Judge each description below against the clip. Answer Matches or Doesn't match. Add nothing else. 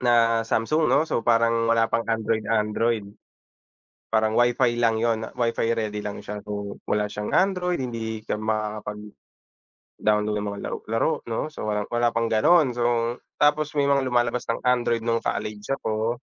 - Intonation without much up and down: Matches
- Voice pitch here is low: Matches